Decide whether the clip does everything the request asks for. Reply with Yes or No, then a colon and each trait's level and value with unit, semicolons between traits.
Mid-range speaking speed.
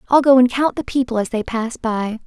No: fast, 265 wpm